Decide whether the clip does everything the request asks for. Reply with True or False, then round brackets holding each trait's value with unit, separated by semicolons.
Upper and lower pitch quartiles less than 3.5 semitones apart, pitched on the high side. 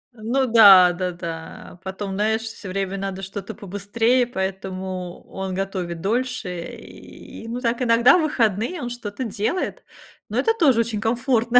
False (4.0 semitones; 210 Hz)